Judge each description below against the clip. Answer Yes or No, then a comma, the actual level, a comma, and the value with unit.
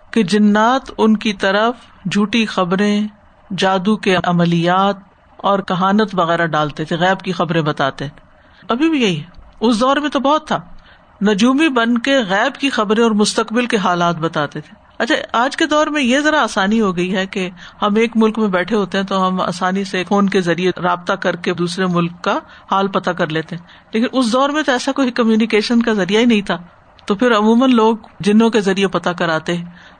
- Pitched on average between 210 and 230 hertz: No, high, 200 Hz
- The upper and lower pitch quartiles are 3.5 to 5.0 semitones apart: Yes, average, 4.1 semitones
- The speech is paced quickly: Yes, fast, 200 wpm